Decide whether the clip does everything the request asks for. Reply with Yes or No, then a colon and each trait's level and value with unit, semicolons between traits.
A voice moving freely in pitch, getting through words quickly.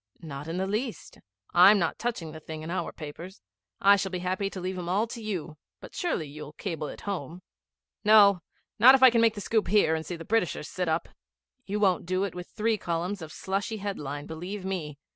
No: average, 4.1 semitones; fast, 220 wpm